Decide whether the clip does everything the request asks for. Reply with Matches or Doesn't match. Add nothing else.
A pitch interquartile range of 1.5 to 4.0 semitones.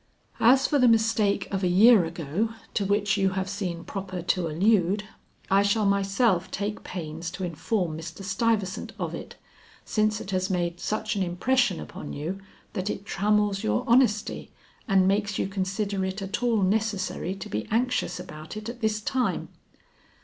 Matches